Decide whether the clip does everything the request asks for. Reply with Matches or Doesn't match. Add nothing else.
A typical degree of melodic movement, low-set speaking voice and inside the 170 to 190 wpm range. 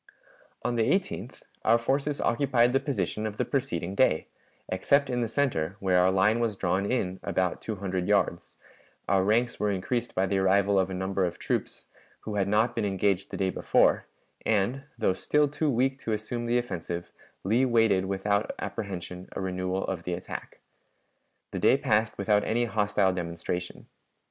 Matches